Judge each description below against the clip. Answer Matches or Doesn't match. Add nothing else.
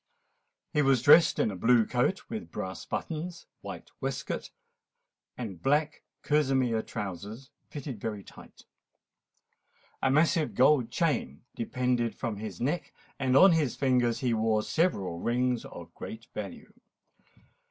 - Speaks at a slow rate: Matches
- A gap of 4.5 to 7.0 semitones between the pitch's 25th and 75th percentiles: Matches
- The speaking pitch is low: Matches